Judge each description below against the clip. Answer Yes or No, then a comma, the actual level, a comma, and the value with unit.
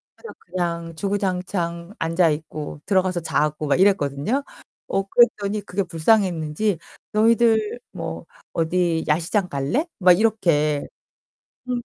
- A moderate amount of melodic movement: Yes, average, 4.2 semitones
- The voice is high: No, medium, 180 Hz